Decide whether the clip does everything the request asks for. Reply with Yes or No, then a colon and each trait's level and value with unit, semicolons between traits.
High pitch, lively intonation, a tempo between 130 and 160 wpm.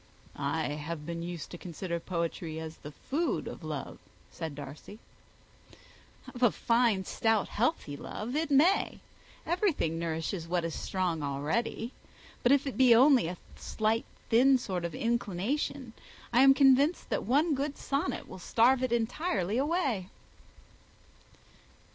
Yes: high, 225 Hz; wide, 7.9 semitones; average, 140 wpm